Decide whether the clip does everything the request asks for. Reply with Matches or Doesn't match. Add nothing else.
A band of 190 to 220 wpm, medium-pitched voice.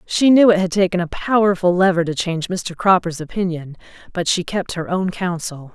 Matches